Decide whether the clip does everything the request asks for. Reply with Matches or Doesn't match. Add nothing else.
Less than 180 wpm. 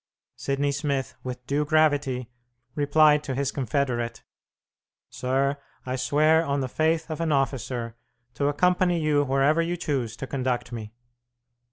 Matches